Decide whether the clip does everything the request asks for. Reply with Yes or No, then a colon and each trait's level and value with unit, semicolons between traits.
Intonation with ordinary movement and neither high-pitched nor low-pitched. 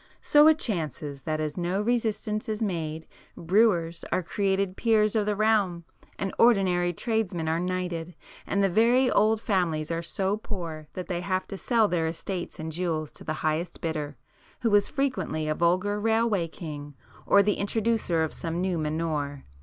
Yes: average, 4.6 semitones; medium, 180 Hz